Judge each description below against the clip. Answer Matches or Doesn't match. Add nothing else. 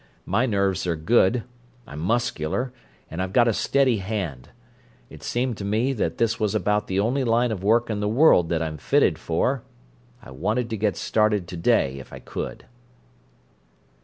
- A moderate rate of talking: Matches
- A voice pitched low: Matches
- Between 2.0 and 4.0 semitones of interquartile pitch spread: Doesn't match